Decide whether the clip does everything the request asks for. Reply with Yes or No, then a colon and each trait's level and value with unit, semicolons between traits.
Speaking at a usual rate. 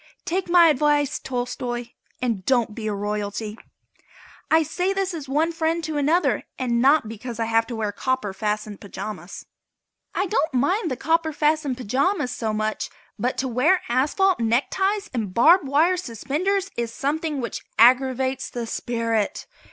Yes: average, 155 wpm